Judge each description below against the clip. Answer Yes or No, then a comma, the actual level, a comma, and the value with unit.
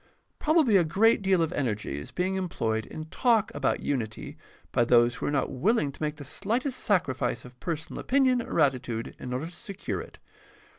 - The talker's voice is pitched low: No, medium, 155 Hz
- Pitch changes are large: Yes, wide, 8.3 semitones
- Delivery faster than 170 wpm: Yes, average, 190 wpm